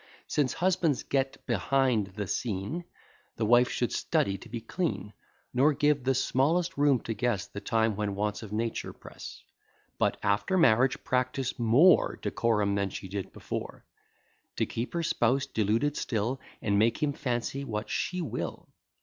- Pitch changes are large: No, average, 4.7 semitones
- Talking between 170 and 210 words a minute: No, average, 160 wpm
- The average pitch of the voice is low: Yes, low, 120 Hz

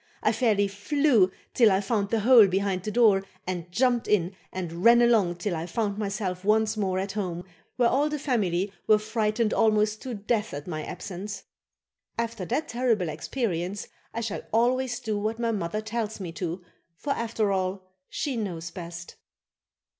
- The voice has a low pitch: No, high, 210 Hz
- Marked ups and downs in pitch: No, average, 3.8 semitones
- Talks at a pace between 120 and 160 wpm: No, average, 170 wpm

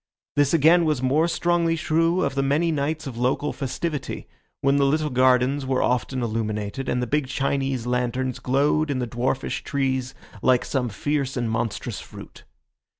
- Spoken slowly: No, average, 165 wpm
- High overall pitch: No, low, 135 Hz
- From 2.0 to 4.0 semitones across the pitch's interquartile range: Yes, average, 3.0 semitones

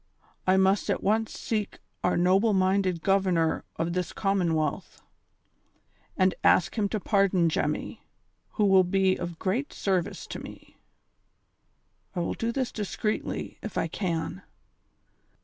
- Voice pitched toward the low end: No, high, 190 Hz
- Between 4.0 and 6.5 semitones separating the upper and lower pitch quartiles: No, average, 2.7 semitones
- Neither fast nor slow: No, slow, 130 wpm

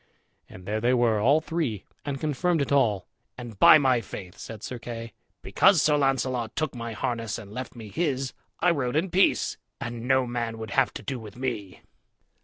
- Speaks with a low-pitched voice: Yes, low, 125 Hz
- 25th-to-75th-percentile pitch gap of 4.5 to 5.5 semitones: No, average, 3.8 semitones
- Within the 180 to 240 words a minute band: Yes, average, 195 wpm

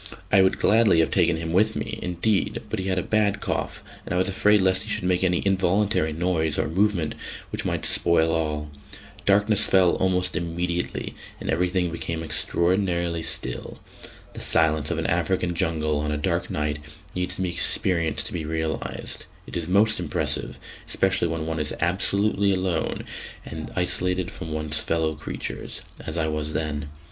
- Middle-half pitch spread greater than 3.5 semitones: No, average, 2.8 semitones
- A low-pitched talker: Yes, very low, 85 Hz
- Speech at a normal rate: Yes, average, 175 wpm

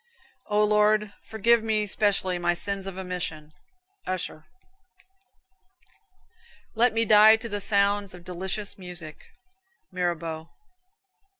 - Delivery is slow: Yes, slow, 105 wpm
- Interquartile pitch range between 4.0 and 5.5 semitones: No, average, 3.0 semitones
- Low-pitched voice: No, high, 200 Hz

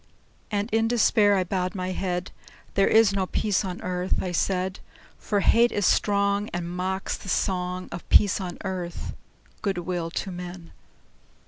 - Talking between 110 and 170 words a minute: Yes, average, 160 wpm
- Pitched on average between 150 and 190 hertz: Yes, medium, 185 Hz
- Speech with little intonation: Yes, narrow, 2.0 semitones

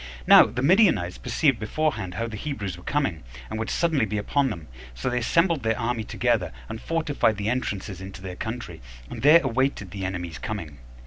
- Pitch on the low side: Yes, low, 110 Hz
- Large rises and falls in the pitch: Yes, wide, 6.2 semitones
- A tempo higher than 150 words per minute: Yes, average, 190 wpm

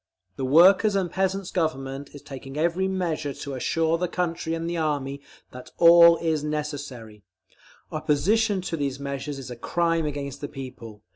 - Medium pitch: Yes, medium, 155 Hz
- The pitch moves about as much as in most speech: Yes, average, 3.7 semitones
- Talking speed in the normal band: Yes, average, 160 wpm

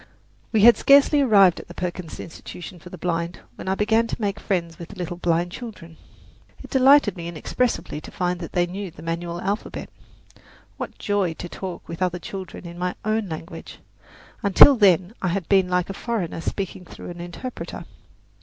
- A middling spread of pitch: Yes, average, 3.0 semitones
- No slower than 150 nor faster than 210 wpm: Yes, average, 185 wpm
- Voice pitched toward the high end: No, medium, 180 Hz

